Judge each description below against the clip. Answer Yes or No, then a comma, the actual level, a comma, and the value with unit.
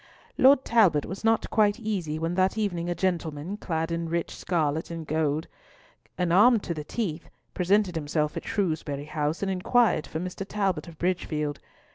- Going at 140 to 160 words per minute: No, average, 170 wpm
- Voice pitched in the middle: Yes, medium, 170 Hz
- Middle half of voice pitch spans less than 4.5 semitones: Yes, average, 3.9 semitones